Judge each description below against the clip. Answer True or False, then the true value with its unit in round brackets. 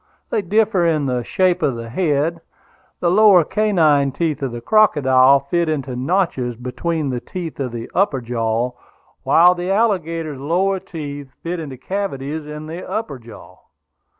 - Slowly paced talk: False (155 wpm)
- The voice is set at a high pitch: False (155 Hz)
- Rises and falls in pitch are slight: False (5.3 semitones)